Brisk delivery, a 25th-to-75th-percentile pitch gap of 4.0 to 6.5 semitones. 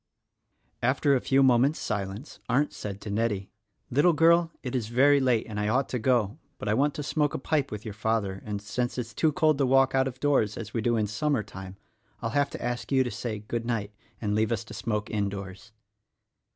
Yes: fast, 225 wpm; average, 4.3 semitones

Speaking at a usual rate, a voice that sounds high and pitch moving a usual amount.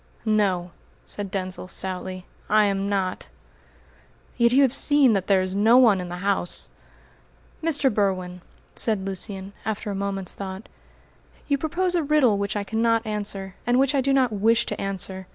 Yes: average, 170 wpm; high, 205 Hz; average, 3.8 semitones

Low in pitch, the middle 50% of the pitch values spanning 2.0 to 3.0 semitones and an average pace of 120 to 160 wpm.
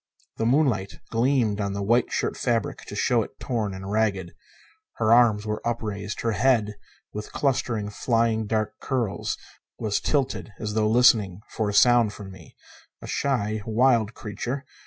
Yes: low, 110 Hz; narrow, 2.5 semitones; average, 155 wpm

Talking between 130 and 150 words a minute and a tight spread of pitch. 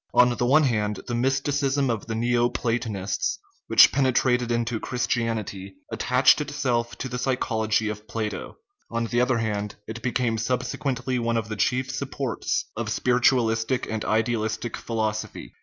Yes: average, 145 wpm; narrow, 2.3 semitones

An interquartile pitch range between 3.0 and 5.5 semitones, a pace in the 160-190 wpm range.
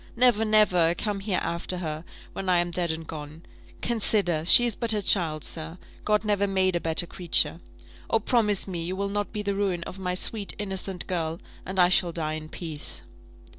No: average, 3.5 semitones; average, 200 wpm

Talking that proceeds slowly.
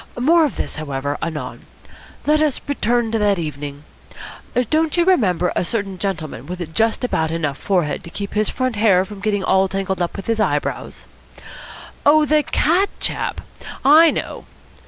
No: average, 170 wpm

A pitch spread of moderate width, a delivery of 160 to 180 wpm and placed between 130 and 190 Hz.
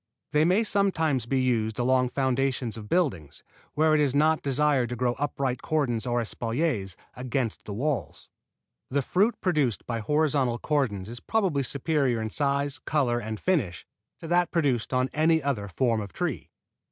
Yes: average, 4.2 semitones; average, 165 wpm; low, 135 Hz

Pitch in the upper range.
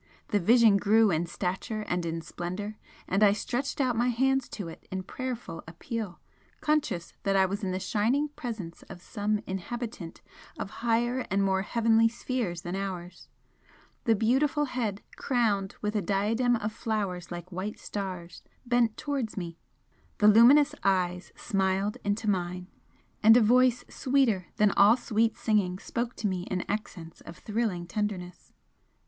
Yes: high, 210 Hz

